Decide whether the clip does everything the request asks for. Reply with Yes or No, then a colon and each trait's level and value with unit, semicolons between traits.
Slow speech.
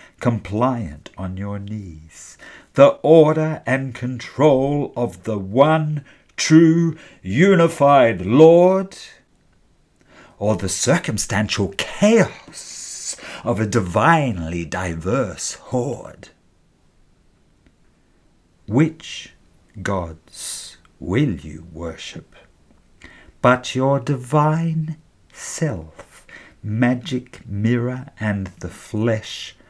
Yes: slow, 75 wpm